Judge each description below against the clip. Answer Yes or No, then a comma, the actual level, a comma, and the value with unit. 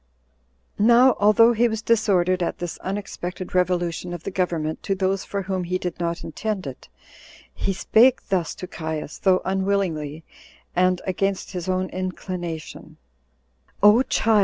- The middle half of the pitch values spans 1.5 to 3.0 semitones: Yes, narrow, 2.6 semitones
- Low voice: No, medium, 185 Hz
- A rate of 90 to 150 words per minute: Yes, average, 145 wpm